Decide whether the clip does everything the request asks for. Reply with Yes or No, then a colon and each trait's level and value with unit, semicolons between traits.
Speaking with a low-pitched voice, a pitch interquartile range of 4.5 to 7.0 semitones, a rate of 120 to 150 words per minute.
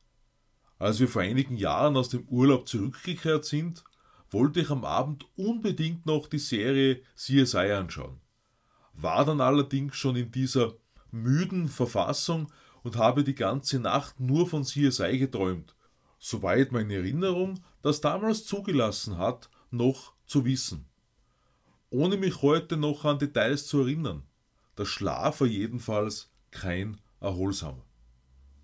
Yes: low, 130 Hz; average, 5.2 semitones; average, 130 wpm